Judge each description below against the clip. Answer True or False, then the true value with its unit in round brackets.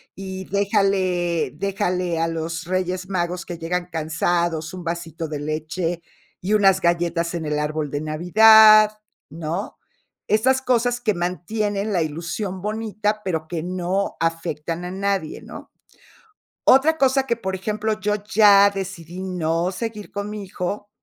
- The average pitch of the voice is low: False (185 Hz)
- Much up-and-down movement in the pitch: False (3.7 semitones)